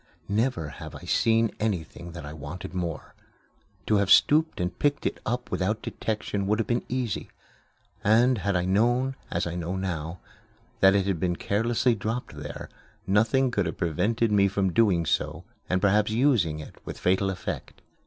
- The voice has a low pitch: Yes, low, 100 Hz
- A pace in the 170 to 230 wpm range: Yes, average, 175 wpm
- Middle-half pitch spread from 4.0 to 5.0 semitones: Yes, average, 4.3 semitones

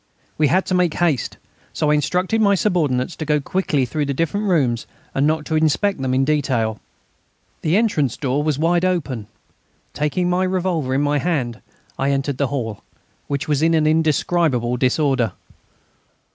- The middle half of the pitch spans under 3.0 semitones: No, average, 4.4 semitones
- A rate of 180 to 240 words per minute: No, average, 165 wpm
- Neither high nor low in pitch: Yes, medium, 150 Hz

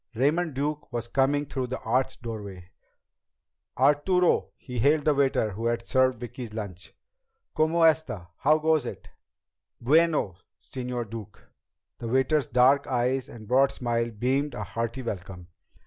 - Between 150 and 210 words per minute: No, average, 140 wpm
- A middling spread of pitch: Yes, average, 3.9 semitones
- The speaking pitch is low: Yes, low, 125 Hz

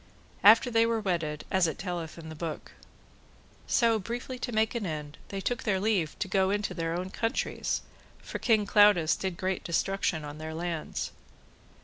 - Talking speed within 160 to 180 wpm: Yes, average, 175 wpm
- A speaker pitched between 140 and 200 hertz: Yes, high, 190 Hz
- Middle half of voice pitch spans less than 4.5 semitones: No, average, 4.9 semitones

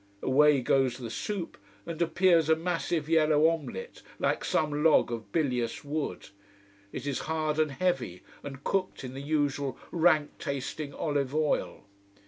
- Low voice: No, medium, 150 Hz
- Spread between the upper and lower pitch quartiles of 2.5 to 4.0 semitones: Yes, average, 2.9 semitones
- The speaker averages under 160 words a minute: Yes, average, 145 wpm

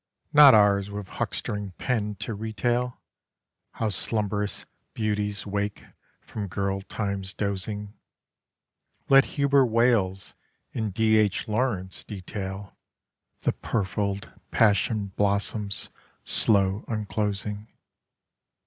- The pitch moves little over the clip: Yes, narrow, 1.9 semitones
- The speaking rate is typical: No, slow, 95 wpm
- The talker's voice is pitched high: No, low, 105 Hz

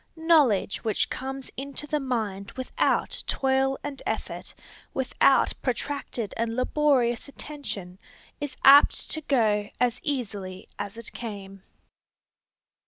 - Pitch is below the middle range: No, very high, 255 Hz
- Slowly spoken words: Yes, slow, 110 wpm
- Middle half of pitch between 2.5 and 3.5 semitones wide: No, average, 4.8 semitones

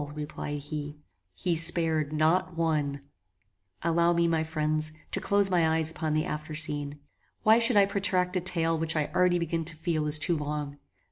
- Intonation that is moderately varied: No, narrow, 2.2 semitones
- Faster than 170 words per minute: Yes, average, 180 wpm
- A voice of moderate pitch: Yes, medium, 160 Hz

